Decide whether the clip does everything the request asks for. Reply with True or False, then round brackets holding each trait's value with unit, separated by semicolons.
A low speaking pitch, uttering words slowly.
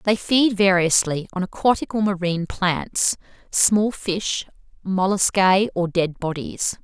False (190 Hz; 125 wpm)